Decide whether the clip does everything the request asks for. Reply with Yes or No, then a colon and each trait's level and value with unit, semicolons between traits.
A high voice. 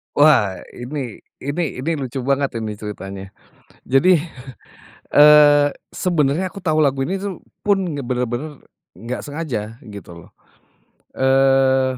No: low, 135 Hz